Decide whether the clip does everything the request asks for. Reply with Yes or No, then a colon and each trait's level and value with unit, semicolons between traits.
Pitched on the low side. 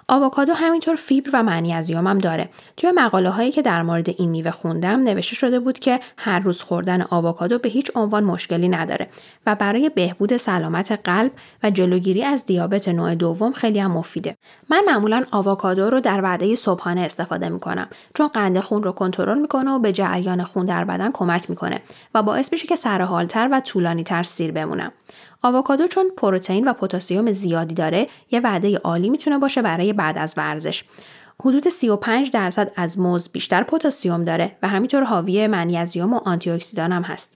No: high, 200 Hz